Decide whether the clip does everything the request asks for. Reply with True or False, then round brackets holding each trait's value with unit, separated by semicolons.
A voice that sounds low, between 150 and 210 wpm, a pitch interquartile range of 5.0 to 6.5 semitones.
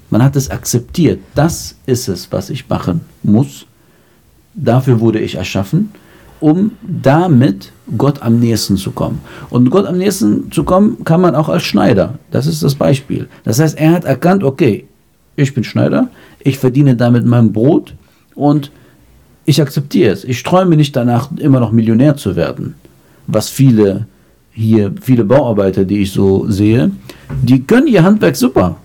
True (125 Hz; 160 wpm; 5.4 semitones)